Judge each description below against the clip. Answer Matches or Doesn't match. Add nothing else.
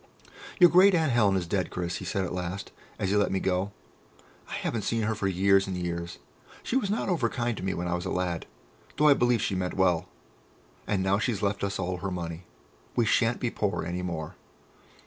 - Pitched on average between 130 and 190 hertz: Doesn't match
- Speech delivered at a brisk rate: Matches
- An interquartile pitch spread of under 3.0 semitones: Doesn't match